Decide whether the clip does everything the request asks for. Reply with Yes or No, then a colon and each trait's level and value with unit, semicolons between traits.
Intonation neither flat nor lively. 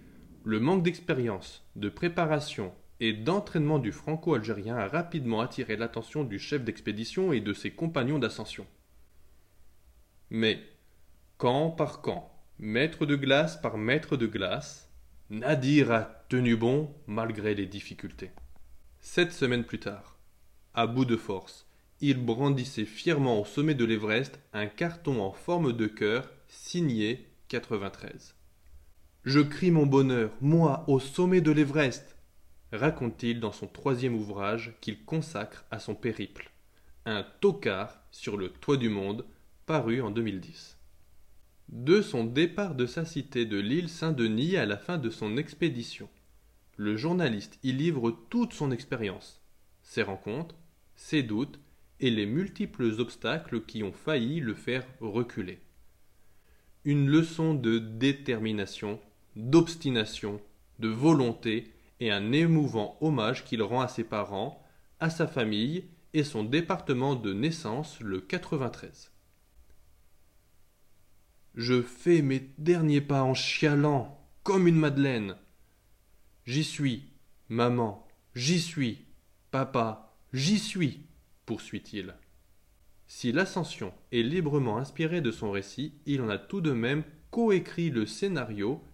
No: wide, 6.8 semitones